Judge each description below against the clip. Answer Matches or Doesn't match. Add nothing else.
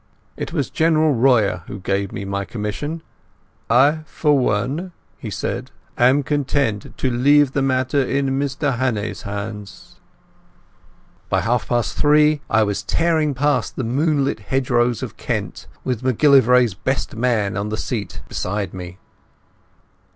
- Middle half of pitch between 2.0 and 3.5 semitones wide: Doesn't match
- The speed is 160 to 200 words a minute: Doesn't match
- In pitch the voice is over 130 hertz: Doesn't match